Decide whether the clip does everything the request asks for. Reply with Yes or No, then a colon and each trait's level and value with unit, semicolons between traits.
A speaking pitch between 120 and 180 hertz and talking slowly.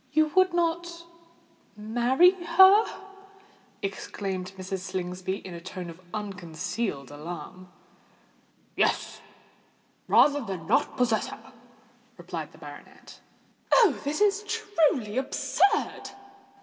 No: high, 225 Hz; slow, 95 wpm